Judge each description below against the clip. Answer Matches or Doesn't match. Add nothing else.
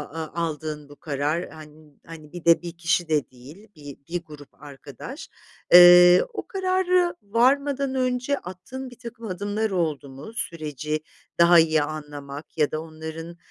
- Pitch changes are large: Matches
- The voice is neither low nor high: Matches